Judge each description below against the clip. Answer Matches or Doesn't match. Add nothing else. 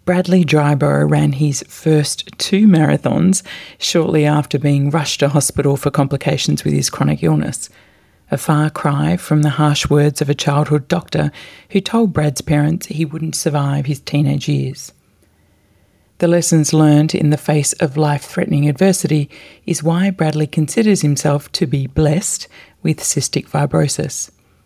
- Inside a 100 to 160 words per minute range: Matches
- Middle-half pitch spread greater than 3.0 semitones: Doesn't match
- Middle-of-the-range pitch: Matches